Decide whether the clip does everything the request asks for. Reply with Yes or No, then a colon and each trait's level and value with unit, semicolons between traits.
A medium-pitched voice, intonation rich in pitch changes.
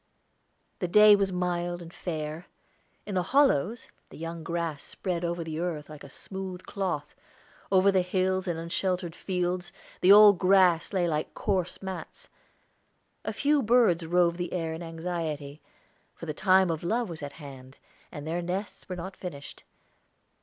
No: medium, 175 Hz; narrow, 2.5 semitones